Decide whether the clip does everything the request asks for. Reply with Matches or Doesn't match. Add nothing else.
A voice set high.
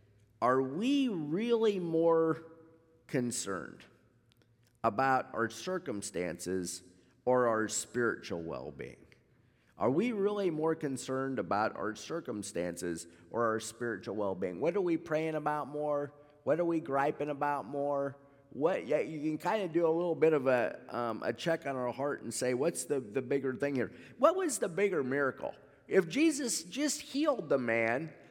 Doesn't match